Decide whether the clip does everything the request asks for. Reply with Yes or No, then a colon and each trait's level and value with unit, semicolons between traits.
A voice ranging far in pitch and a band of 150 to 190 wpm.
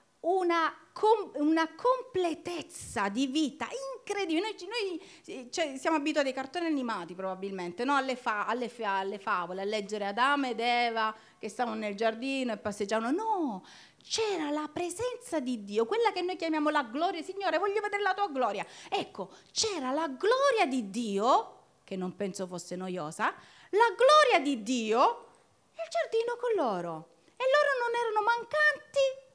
Yes: wide, 9.0 semitones; average, 155 wpm